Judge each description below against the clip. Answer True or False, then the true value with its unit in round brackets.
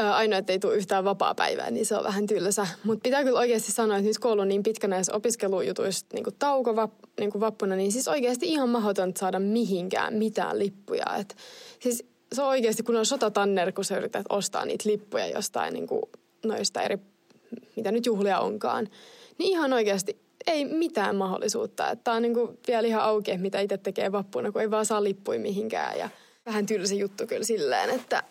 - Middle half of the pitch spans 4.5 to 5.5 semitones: False (3.0 semitones)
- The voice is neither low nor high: False (215 Hz)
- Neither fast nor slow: False (190 wpm)